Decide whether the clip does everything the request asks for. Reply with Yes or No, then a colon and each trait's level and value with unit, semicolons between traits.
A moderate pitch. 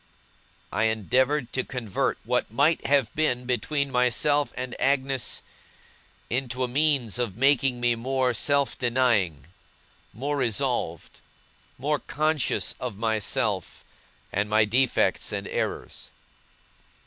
No: low, 125 Hz